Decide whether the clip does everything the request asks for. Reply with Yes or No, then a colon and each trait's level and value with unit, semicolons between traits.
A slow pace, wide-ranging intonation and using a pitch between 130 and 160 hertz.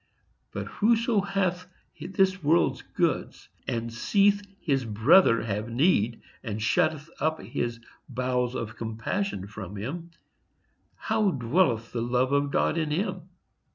Yes: slow, 125 wpm; wide, 8.1 semitones; medium, 140 Hz